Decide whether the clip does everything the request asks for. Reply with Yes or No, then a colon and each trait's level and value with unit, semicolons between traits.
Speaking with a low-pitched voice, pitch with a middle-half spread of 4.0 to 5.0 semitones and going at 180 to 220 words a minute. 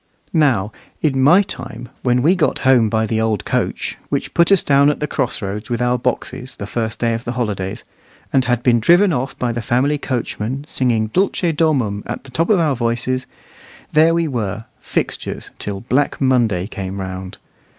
Yes: low, 125 Hz; average, 4.4 semitones; average, 190 wpm